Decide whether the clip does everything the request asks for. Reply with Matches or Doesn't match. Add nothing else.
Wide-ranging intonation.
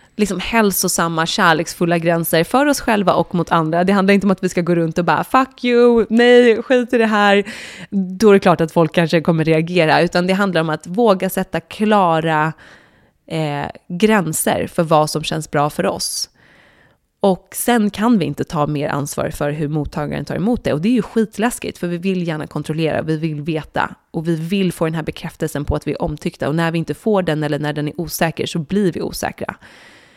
Doesn't match